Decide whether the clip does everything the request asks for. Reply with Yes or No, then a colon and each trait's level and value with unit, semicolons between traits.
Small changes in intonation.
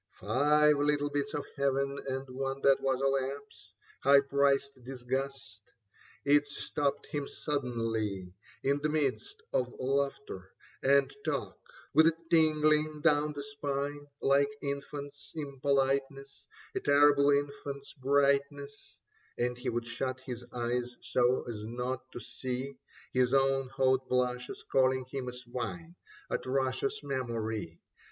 Yes: narrow, 2.0 semitones